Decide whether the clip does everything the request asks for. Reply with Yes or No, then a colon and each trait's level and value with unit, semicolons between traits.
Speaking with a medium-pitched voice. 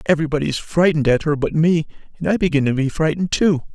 Yes: medium, 155 Hz